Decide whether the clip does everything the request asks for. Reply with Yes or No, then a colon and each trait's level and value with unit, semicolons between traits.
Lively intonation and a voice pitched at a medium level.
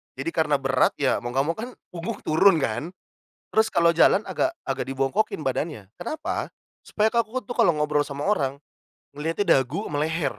Yes: wide, 6.3 semitones; medium, 160 Hz